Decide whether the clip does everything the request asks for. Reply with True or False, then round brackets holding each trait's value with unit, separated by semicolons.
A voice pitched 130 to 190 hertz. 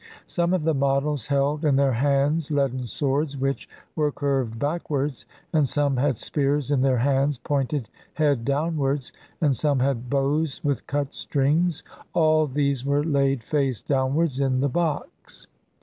True (140 Hz)